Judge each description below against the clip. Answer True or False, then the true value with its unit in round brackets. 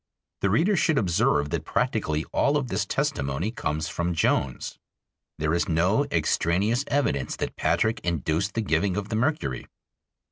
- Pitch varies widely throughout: True (6.1 semitones)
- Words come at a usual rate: True (150 wpm)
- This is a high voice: False (95 Hz)